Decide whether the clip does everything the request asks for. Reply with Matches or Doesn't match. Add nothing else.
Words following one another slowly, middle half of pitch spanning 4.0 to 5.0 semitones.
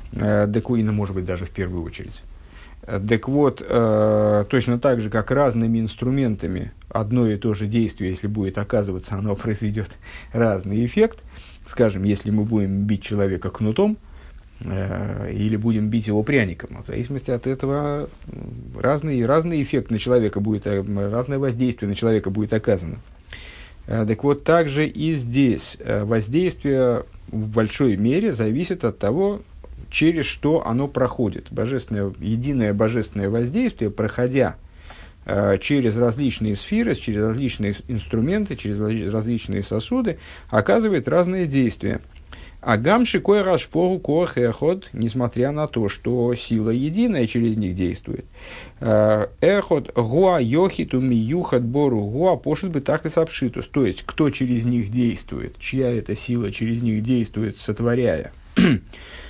Doesn't match